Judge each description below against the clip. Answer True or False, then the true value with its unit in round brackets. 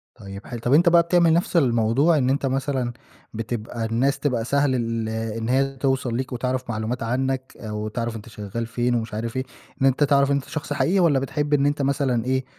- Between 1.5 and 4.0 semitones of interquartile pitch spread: True (3.3 semitones)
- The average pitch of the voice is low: True (130 Hz)